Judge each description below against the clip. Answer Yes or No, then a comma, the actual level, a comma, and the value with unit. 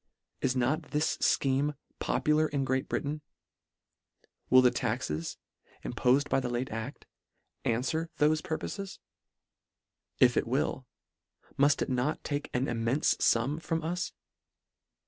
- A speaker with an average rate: No, slow, 130 wpm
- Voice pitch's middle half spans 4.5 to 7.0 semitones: No, average, 3.5 semitones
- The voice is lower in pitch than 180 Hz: Yes, medium, 140 Hz